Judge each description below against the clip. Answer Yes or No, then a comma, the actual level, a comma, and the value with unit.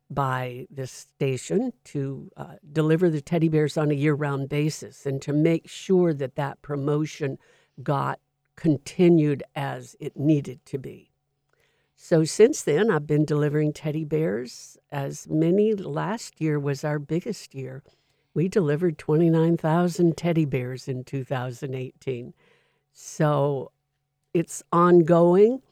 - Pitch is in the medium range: Yes, medium, 150 Hz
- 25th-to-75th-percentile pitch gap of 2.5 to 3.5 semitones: Yes, average, 3.0 semitones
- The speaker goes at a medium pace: No, slow, 125 wpm